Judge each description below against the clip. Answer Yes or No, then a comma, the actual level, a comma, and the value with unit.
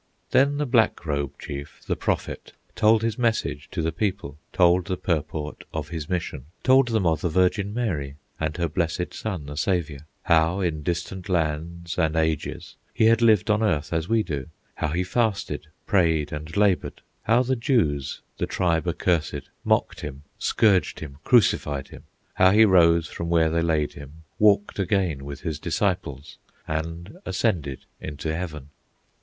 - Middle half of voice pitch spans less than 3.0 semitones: No, average, 4.6 semitones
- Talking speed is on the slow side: No, average, 165 wpm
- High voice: No, very low, 85 Hz